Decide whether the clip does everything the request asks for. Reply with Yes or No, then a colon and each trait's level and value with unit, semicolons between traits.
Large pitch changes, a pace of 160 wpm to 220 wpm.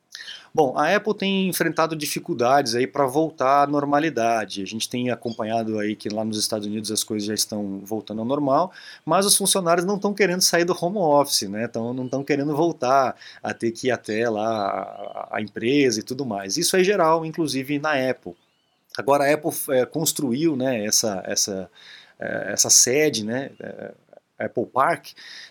Yes: wide, 6.6 semitones; average, 180 wpm